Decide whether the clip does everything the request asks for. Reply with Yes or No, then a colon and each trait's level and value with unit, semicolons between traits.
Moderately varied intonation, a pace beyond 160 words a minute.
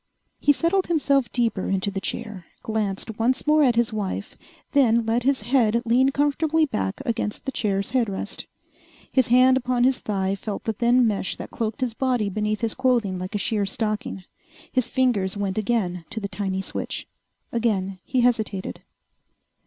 Yes: average, 4.1 semitones; average, 170 wpm